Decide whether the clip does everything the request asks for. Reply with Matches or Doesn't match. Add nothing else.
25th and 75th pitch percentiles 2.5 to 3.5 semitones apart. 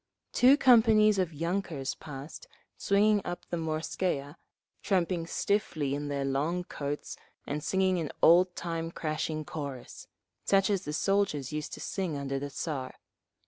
Doesn't match